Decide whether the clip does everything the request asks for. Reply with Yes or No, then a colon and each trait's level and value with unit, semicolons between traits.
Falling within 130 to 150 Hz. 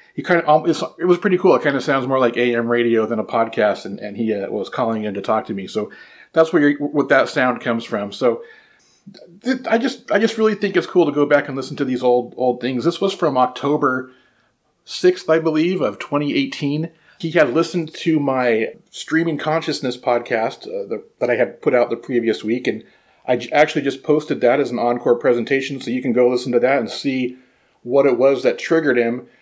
Yes: medium, 140 Hz